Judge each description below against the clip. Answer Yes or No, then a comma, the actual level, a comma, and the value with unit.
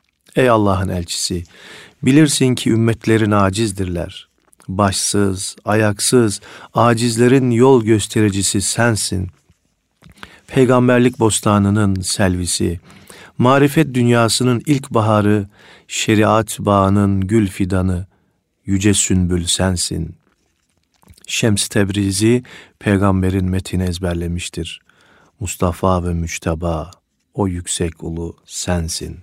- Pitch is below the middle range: Yes, low, 100 Hz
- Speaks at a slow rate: Yes, slow, 80 wpm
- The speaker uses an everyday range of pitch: Yes, average, 3.6 semitones